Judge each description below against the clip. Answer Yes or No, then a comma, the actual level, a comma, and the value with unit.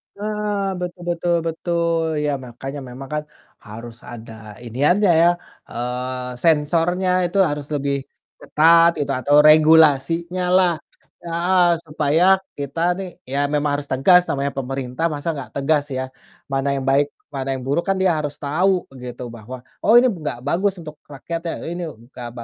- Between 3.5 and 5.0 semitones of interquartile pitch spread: Yes, average, 4.2 semitones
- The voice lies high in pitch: No, medium, 150 Hz